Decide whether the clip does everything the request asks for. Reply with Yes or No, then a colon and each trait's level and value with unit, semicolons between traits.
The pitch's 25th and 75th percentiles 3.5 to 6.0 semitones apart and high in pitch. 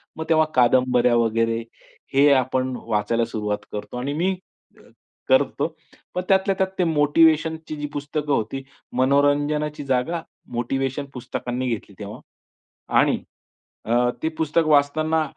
No: average, 4.2 semitones; medium, 140 Hz